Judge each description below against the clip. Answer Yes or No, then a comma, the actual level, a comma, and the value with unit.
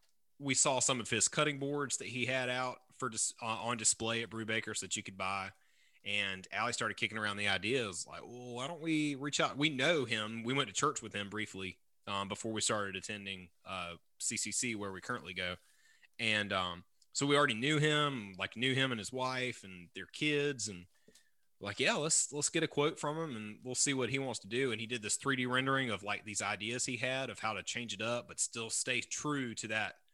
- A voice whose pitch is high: No, low, 115 Hz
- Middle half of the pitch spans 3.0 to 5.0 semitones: Yes, average, 4.2 semitones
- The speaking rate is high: Yes, fast, 235 wpm